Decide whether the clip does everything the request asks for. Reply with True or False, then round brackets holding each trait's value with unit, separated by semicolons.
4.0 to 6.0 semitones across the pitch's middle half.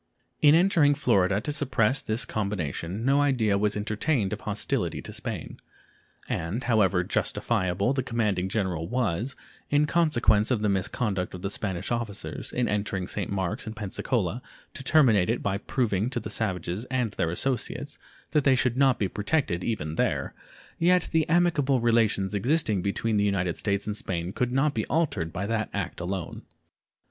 True (5.1 semitones)